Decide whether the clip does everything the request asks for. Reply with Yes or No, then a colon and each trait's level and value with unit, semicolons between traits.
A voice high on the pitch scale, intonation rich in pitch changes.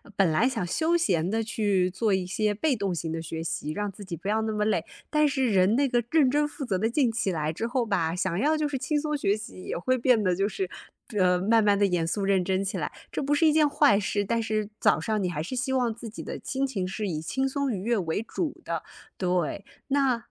Yes: high, 210 Hz; wide, 5.8 semitones